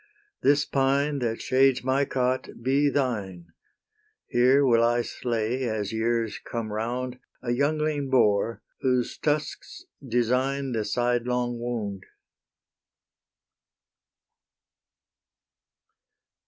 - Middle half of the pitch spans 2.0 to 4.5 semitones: Yes, average, 2.7 semitones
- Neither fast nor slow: No, slow, 95 wpm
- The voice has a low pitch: Yes, low, 125 Hz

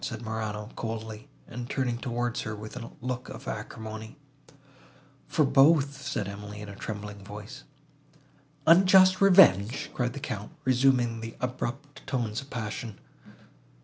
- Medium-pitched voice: No, low, 120 Hz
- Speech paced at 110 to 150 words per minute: Yes, slow, 135 wpm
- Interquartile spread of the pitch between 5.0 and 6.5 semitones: No, average, 3.9 semitones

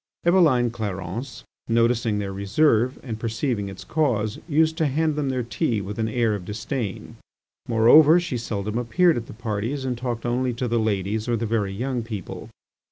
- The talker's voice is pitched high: No, low, 115 Hz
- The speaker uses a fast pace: No, average, 175 wpm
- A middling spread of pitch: Yes, average, 3.5 semitones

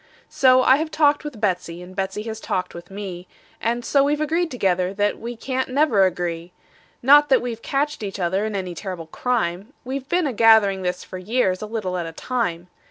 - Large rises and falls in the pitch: Yes, wide, 6.1 semitones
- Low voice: No, high, 215 Hz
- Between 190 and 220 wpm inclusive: Yes, fast, 205 wpm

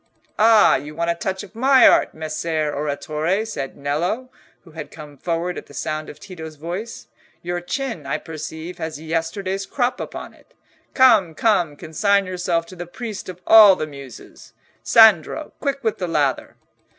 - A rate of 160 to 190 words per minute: Yes, average, 165 wpm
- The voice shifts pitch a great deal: No, average, 4.9 semitones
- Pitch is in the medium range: Yes, medium, 170 Hz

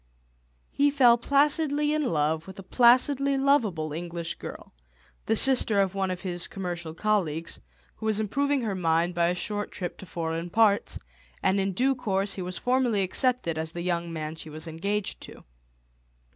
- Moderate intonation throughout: No, wide, 6.4 semitones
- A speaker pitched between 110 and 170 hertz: No, high, 195 Hz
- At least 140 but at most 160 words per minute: No, average, 170 wpm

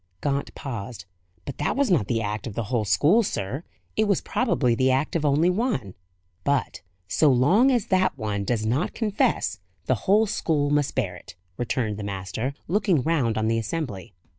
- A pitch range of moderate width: No, wide, 7.3 semitones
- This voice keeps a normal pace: Yes, average, 185 wpm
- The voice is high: No, low, 130 Hz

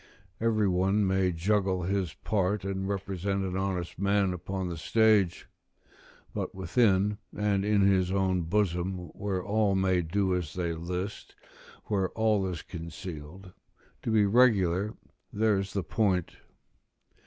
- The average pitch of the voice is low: Yes, very low, 95 Hz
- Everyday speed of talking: No, slow, 130 wpm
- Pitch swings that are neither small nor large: No, narrow, 2.0 semitones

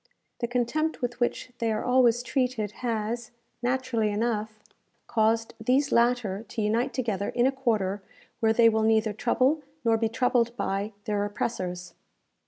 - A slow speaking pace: No, average, 150 wpm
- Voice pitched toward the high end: Yes, high, 230 Hz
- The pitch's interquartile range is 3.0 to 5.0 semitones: No, narrow, 2.4 semitones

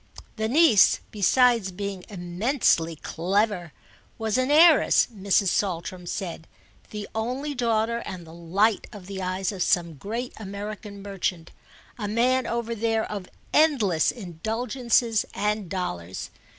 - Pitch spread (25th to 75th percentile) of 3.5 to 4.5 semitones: Yes, average, 4.1 semitones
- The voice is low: No, high, 205 Hz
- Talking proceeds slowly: Yes, slow, 125 wpm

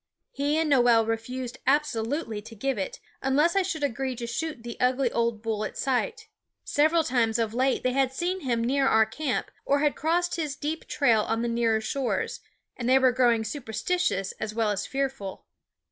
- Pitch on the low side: No, very high, 255 Hz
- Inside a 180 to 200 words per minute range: Yes, average, 190 wpm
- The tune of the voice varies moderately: Yes, average, 4.2 semitones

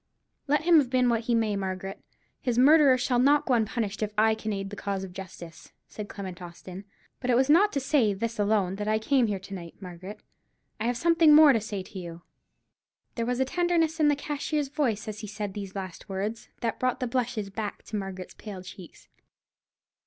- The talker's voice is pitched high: Yes, high, 220 Hz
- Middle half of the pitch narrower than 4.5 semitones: No, average, 5.0 semitones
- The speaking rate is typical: No, fast, 210 wpm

